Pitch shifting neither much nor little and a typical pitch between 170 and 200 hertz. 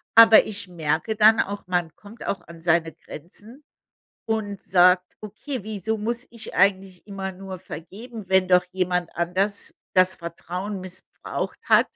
Yes: average, 3.1 semitones; high, 190 Hz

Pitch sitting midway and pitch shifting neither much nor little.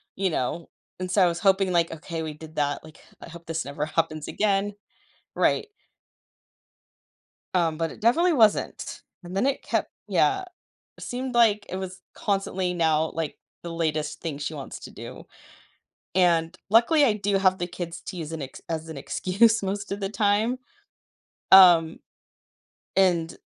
Yes: medium, 180 Hz; average, 3.8 semitones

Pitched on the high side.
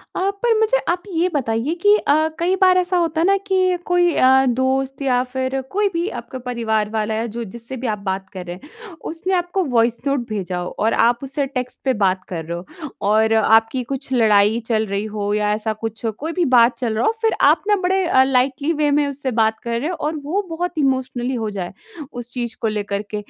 Yes: very high, 255 Hz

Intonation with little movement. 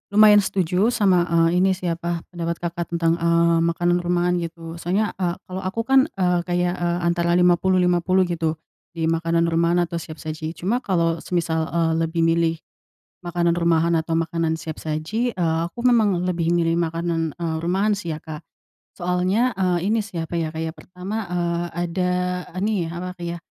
Yes: narrow, 1.6 semitones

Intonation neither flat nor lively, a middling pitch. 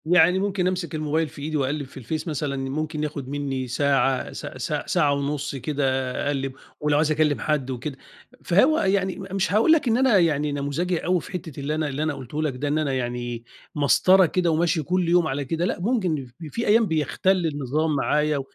Yes: average, 4.1 semitones; medium, 150 Hz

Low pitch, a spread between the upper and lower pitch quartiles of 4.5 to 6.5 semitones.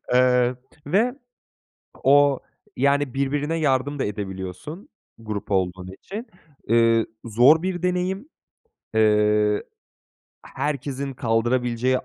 Yes: low, 130 Hz; average, 4.9 semitones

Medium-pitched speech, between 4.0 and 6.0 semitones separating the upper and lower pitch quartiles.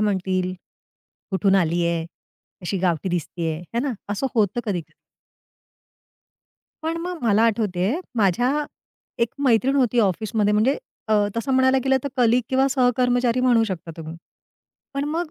No: high, 225 Hz; wide, 5.5 semitones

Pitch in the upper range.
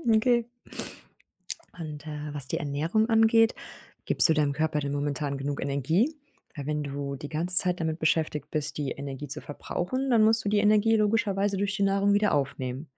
No: medium, 160 Hz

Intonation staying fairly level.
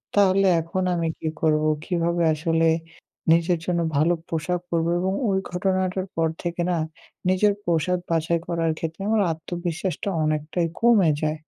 Yes: narrow, 2.2 semitones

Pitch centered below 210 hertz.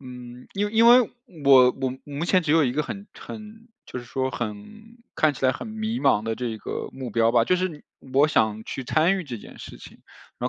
Yes: medium, 140 Hz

